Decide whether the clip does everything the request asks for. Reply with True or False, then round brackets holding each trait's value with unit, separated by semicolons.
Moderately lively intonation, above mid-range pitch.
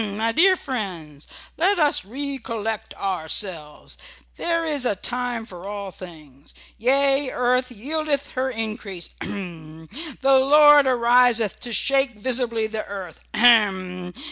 False (5.7 semitones; 230 Hz)